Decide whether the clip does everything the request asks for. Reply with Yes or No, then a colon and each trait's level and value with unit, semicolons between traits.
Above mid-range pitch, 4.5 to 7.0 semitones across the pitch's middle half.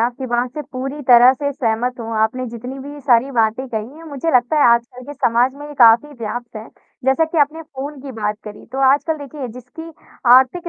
No: very high, 255 Hz; average, 3.3 semitones